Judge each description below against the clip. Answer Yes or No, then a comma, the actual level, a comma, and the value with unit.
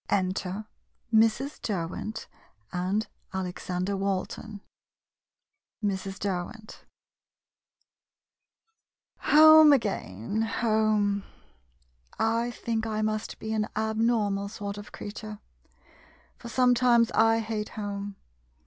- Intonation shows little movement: Yes, narrow, 2.1 semitones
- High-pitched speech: Yes, high, 215 Hz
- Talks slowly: Yes, slow, 90 wpm